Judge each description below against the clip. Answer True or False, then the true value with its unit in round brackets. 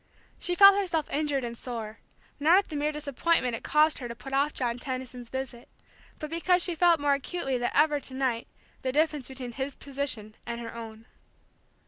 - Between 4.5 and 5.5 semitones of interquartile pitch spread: False (4.0 semitones)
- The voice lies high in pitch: True (275 Hz)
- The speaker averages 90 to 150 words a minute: False (190 wpm)